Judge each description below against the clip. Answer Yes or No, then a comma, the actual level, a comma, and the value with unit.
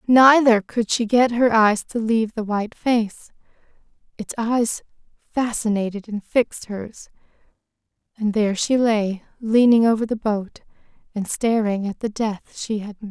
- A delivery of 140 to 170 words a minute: Yes, average, 150 wpm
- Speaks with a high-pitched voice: Yes, high, 220 Hz